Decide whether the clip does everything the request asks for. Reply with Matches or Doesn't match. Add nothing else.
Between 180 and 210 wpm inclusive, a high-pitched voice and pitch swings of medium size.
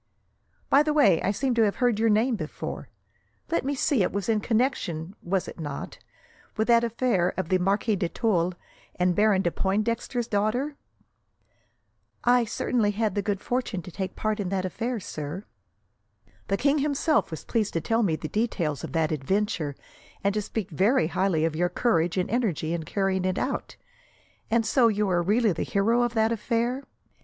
Matches